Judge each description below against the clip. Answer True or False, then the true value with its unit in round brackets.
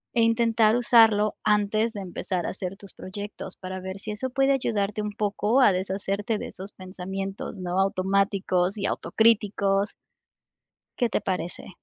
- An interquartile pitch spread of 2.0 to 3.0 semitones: True (2.4 semitones)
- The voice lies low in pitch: False (200 Hz)